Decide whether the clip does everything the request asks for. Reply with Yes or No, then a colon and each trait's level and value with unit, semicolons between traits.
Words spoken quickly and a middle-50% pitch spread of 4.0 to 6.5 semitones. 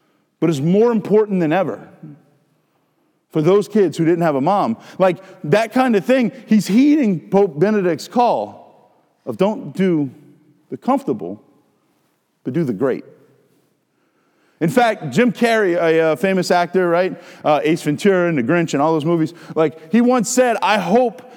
No: average, 165 wpm; wide, 5.6 semitones